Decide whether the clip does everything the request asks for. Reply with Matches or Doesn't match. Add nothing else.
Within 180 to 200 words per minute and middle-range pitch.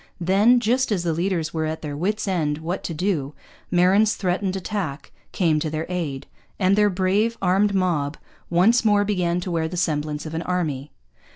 Matches